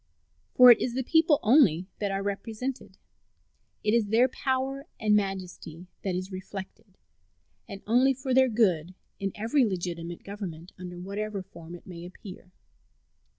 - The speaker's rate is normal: Yes, average, 150 wpm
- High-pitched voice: Yes, high, 200 Hz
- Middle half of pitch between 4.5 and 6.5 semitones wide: Yes, average, 5.1 semitones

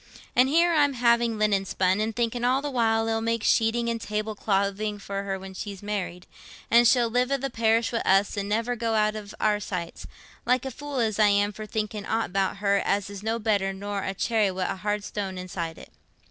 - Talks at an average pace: No, fast, 220 wpm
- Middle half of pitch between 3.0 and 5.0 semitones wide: No, narrow, 2.6 semitones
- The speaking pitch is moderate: No, high, 215 Hz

